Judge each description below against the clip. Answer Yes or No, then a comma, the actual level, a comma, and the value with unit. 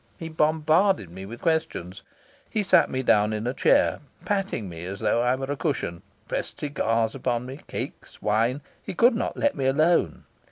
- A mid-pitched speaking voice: No, low, 130 Hz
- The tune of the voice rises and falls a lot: Yes, wide, 6.6 semitones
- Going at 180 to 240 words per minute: Yes, average, 185 wpm